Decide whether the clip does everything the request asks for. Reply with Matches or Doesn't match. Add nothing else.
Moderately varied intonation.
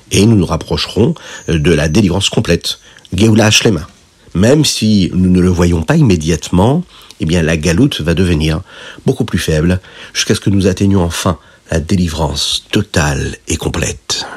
Matches